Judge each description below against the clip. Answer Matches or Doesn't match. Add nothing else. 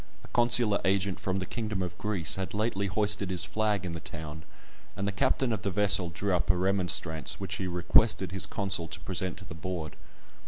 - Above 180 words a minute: Matches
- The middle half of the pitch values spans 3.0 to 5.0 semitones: Doesn't match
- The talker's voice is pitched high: Doesn't match